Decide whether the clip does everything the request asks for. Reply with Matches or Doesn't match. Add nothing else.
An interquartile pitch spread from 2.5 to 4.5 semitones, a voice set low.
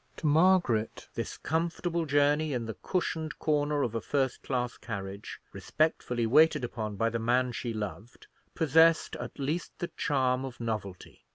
Doesn't match